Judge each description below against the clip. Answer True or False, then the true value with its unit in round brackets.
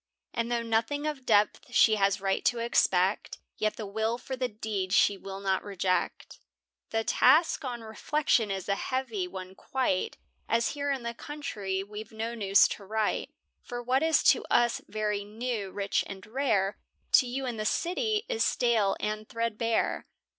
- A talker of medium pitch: False (220 Hz)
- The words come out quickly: False (175 wpm)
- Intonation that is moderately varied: True (3.8 semitones)